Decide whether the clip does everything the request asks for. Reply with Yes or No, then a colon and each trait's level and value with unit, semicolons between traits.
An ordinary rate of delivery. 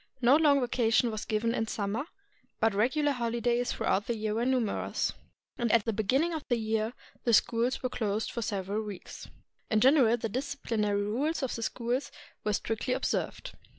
Yes: average, 180 wpm